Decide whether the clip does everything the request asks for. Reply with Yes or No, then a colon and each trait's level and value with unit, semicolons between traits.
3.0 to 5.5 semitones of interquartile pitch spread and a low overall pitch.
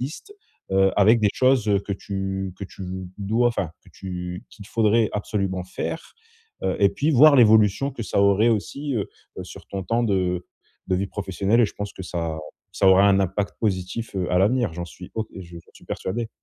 Yes: average, 3.3 semitones; low, 100 Hz